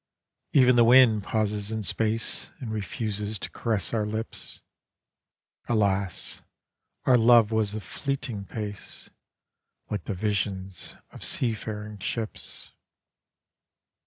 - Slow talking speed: Yes, slow, 105 wpm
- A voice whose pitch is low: Yes, low, 110 Hz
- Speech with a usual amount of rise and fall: No, narrow, 2.0 semitones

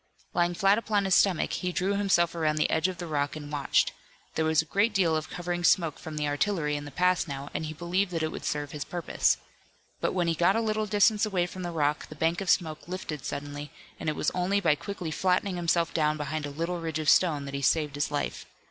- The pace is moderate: No, fast, 245 wpm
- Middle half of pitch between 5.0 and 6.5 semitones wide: No, average, 3.4 semitones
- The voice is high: No, medium, 165 Hz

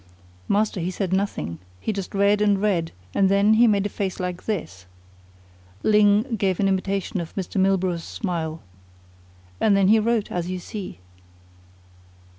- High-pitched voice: Yes, high, 195 Hz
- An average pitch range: No, narrow, 2.3 semitones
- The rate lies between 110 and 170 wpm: Yes, average, 155 wpm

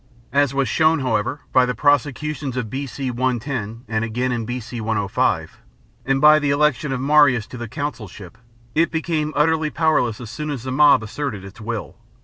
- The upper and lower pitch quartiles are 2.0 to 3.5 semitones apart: No, average, 4.4 semitones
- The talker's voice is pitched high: No, low, 130 Hz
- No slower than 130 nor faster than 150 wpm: No, average, 175 wpm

